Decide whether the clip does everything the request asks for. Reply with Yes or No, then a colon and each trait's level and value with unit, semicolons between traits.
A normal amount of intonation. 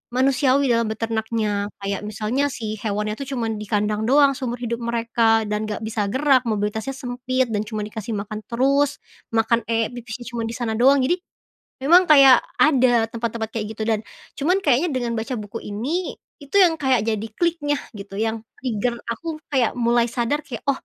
Yes: average, 3.5 semitones